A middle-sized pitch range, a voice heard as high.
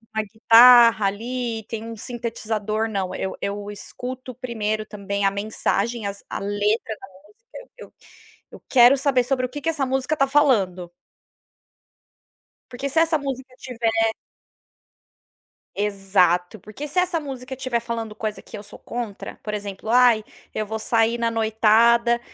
Yes: average, 3.4 semitones; high, 230 Hz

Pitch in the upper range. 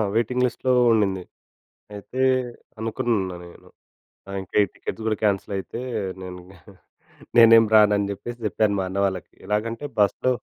No: low, 105 Hz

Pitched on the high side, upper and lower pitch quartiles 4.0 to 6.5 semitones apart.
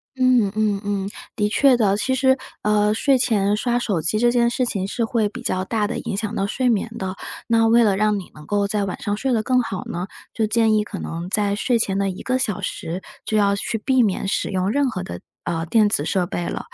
No: high, 210 Hz; average, 3.2 semitones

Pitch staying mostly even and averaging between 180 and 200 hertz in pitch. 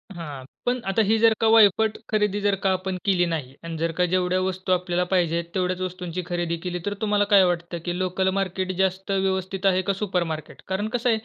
Yes: narrow, 1.9 semitones; medium, 185 Hz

